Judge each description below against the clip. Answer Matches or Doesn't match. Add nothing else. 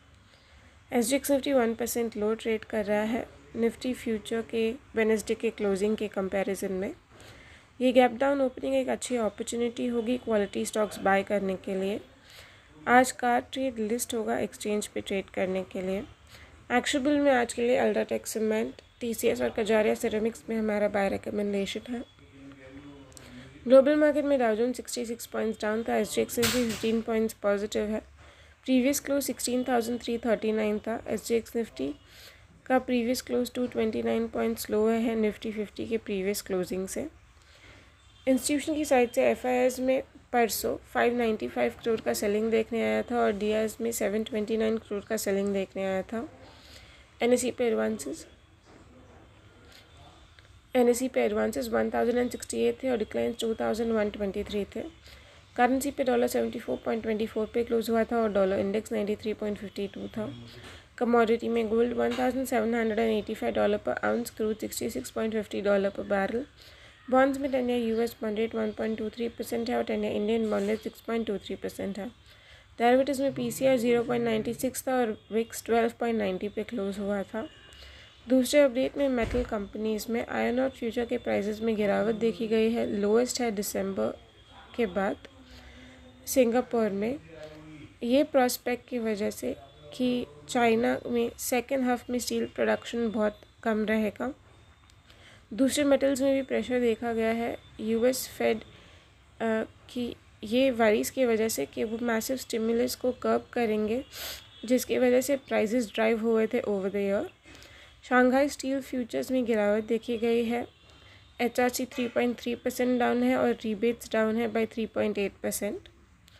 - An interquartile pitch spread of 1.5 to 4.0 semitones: Matches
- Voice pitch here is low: Doesn't match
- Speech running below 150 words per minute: Doesn't match